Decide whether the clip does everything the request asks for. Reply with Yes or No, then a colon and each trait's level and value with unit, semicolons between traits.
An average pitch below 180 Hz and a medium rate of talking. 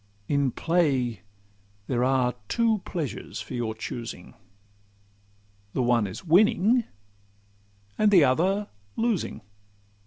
No: medium, 140 Hz; slow, 100 wpm